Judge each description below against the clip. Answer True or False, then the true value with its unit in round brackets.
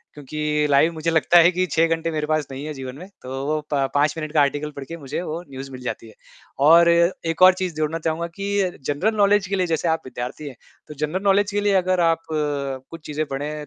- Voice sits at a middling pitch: True (155 Hz)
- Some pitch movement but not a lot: True (3.0 semitones)